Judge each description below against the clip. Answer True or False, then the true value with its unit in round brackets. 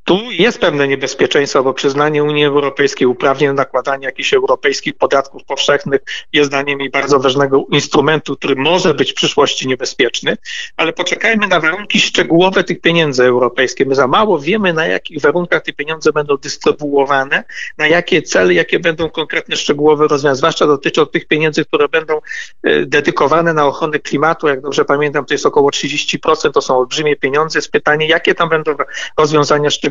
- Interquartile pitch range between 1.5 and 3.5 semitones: True (2.4 semitones)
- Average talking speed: False (165 wpm)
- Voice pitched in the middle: True (150 Hz)